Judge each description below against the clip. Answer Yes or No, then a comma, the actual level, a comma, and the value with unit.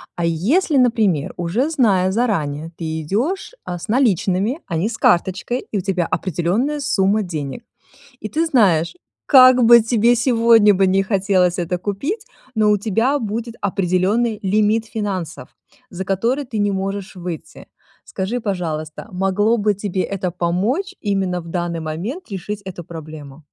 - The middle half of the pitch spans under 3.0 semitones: No, average, 4.5 semitones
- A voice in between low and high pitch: No, high, 200 Hz